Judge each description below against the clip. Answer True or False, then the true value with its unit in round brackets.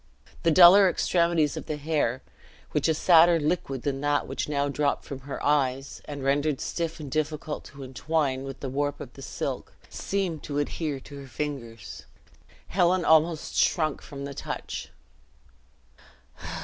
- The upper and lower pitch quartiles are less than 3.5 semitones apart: True (2.7 semitones)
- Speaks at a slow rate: False (155 wpm)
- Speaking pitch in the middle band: True (145 Hz)